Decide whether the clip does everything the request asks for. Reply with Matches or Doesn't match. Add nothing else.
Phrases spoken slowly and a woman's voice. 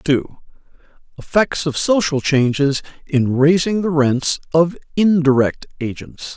Doesn't match